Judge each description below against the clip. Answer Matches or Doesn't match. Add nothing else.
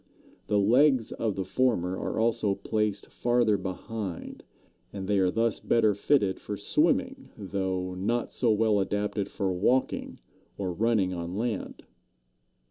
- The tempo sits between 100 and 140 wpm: Matches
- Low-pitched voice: Matches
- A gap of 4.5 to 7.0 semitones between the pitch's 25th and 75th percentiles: Doesn't match